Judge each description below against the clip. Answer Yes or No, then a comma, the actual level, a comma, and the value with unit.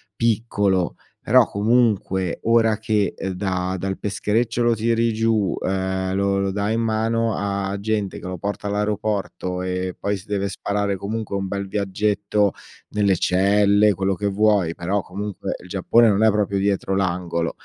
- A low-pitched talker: Yes, low, 100 Hz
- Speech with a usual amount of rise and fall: No, narrow, 2.0 semitones